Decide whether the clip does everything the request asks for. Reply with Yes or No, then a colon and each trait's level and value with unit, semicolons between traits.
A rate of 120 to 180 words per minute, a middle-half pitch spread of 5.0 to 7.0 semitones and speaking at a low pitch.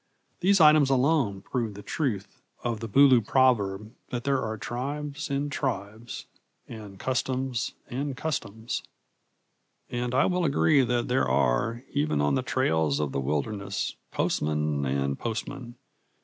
Yes: slow, 135 wpm; wide, 5.6 semitones; low, 120 Hz